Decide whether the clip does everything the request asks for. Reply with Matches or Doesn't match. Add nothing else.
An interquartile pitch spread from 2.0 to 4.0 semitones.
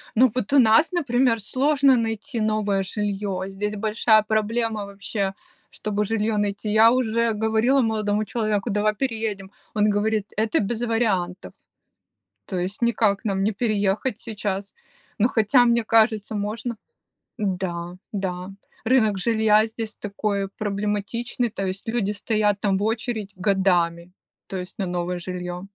Matches